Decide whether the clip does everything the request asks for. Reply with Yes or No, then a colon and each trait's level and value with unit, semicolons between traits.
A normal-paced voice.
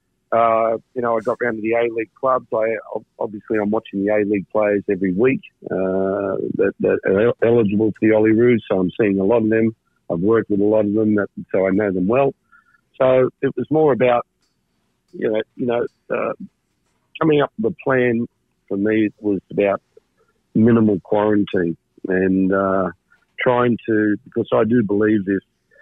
Yes: average, 190 wpm